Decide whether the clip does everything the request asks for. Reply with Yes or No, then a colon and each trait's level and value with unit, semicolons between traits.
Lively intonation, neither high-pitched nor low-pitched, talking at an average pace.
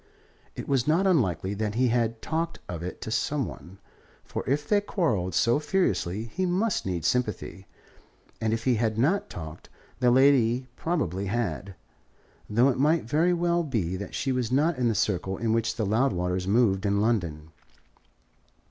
No: wide, 6.5 semitones; low, 115 Hz; average, 170 wpm